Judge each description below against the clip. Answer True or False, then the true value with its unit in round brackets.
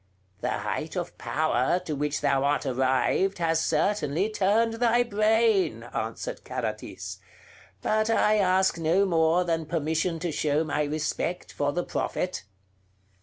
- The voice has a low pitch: False (170 Hz)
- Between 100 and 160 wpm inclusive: True (135 wpm)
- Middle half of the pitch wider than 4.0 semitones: True (5.3 semitones)